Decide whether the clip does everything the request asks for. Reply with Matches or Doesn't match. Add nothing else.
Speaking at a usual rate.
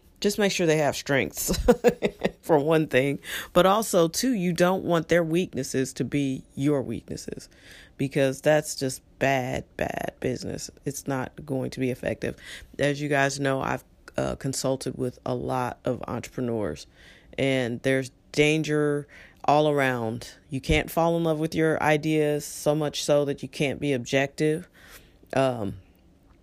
Matches